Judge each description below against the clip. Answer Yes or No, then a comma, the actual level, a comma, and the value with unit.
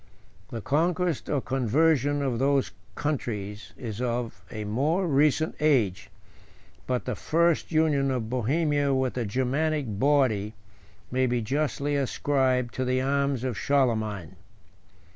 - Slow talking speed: Yes, slow, 125 wpm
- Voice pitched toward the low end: Yes, low, 130 Hz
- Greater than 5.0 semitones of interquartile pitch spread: No, average, 3.7 semitones